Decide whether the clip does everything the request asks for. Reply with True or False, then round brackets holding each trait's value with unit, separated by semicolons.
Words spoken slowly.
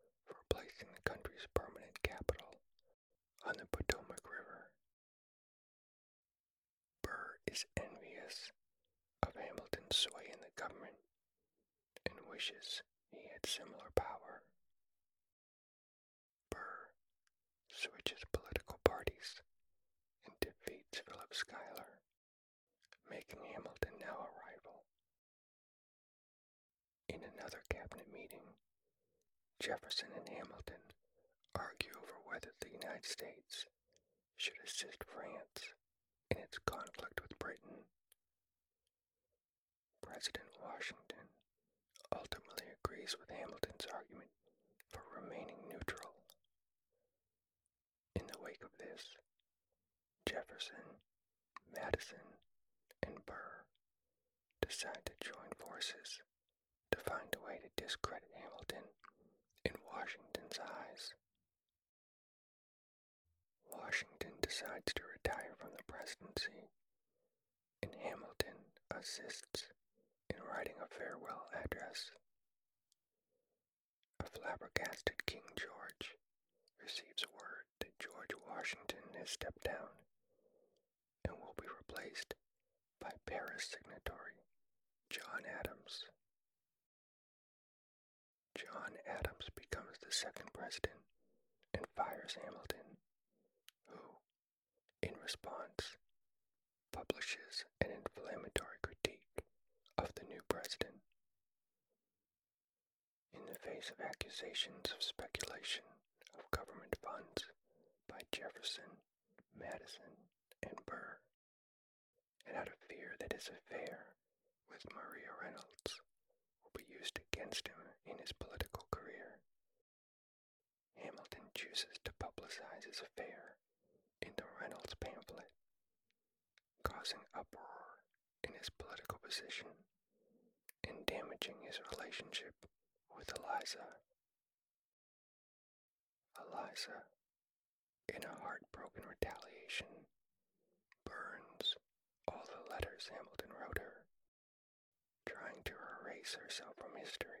True (90 wpm)